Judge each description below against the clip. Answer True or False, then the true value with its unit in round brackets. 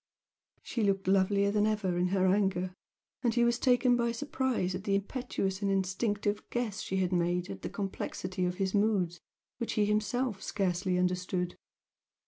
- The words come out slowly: False (165 wpm)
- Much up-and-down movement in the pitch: False (2.8 semitones)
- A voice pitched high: True (195 Hz)